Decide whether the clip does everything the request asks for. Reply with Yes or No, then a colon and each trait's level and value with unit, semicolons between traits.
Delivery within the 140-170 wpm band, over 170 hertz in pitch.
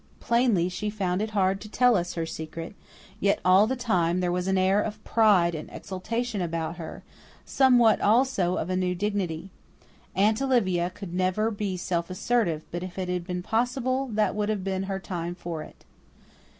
No: average, 185 wpm; high, 190 Hz